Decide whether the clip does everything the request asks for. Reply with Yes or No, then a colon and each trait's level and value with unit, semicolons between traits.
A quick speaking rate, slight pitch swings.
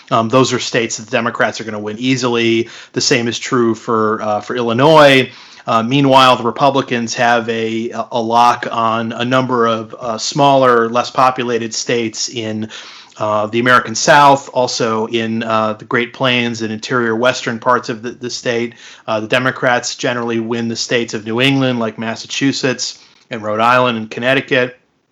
Yes: fast, 175 wpm; narrow, 2.0 semitones